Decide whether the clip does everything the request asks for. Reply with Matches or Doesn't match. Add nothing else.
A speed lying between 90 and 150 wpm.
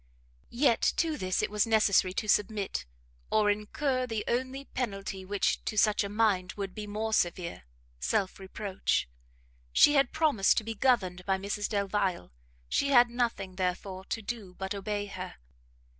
Doesn't match